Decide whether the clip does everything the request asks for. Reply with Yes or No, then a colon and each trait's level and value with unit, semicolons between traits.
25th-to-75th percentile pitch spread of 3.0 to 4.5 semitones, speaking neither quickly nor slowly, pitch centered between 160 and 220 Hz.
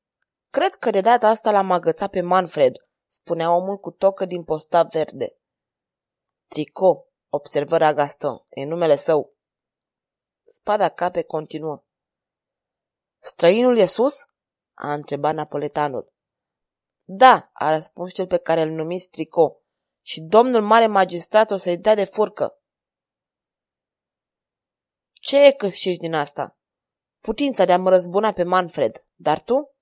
No: wide, 5.4 semitones; average, 125 wpm; medium, 180 Hz